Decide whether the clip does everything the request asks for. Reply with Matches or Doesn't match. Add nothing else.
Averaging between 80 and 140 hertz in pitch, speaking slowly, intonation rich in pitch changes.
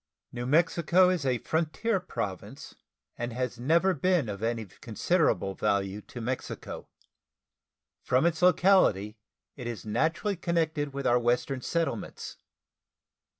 Matches